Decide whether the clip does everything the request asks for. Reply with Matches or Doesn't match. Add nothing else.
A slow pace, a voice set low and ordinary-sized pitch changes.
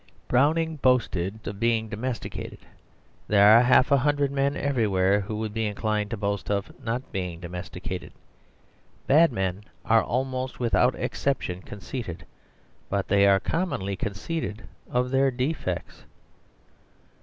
Matches